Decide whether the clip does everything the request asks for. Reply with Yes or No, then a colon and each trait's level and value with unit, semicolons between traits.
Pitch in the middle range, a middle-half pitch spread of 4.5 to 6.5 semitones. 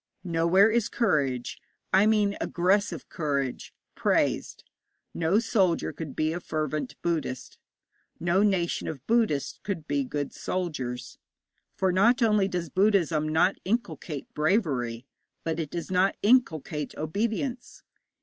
Yes: medium, 170 Hz; average, 5.1 semitones